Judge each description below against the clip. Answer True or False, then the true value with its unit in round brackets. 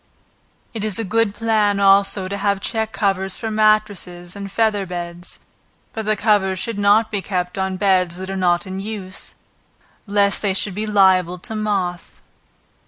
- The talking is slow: False (170 wpm)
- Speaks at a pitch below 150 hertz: False (200 Hz)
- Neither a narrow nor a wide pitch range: False (2.2 semitones)